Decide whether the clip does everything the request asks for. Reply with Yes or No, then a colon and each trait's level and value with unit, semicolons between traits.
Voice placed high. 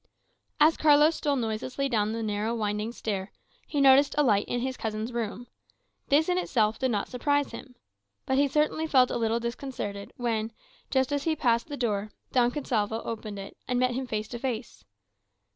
Yes: high, 240 Hz